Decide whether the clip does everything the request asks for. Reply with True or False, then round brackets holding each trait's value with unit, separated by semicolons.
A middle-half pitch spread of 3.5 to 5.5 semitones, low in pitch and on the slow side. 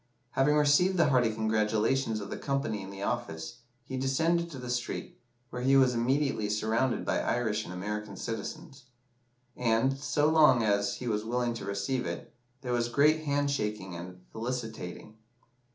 False (4.2 semitones; 120 Hz; 165 wpm)